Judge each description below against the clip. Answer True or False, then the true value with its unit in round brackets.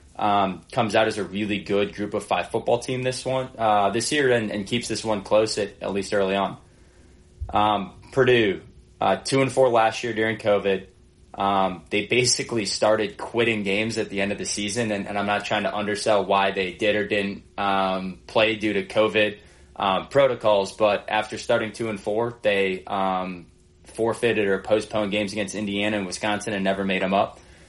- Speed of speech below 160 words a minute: False (195 wpm)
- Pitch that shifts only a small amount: True (2.2 semitones)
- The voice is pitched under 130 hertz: True (105 Hz)